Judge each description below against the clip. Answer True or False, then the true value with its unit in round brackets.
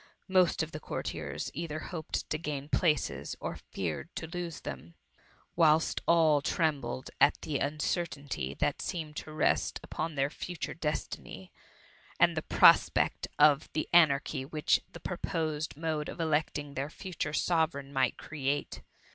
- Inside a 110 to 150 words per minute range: True (145 wpm)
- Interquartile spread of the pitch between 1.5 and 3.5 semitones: True (2.5 semitones)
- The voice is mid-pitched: True (155 Hz)